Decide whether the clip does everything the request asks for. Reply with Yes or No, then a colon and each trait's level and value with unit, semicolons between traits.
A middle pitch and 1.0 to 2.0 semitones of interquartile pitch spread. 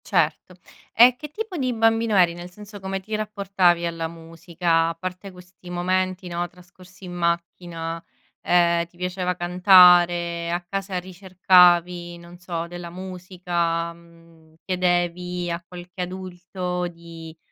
Yes: medium, 180 Hz; narrow, 1.4 semitones